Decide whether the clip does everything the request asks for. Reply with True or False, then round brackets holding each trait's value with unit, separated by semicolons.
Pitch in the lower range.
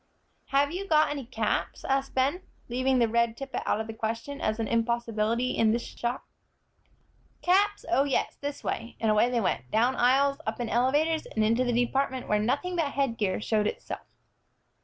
False (245 Hz)